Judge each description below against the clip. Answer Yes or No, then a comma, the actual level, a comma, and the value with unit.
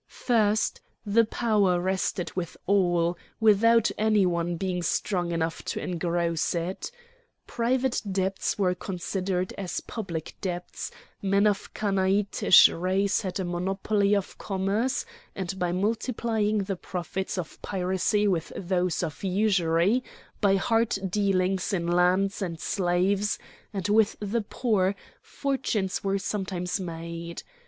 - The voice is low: No, high, 190 Hz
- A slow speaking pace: Yes, slow, 125 wpm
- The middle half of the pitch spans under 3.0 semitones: Yes, narrow, 2.6 semitones